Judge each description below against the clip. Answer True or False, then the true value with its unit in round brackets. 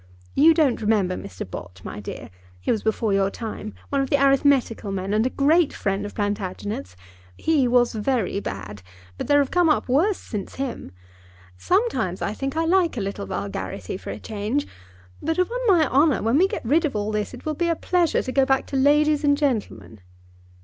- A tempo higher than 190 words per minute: True (200 wpm)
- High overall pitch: True (250 Hz)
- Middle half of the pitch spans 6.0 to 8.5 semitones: True (6.7 semitones)